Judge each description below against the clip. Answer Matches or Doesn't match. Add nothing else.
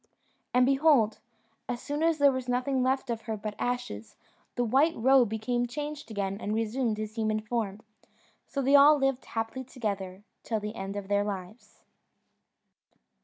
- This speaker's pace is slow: Doesn't match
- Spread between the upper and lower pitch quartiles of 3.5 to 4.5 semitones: Matches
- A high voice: Matches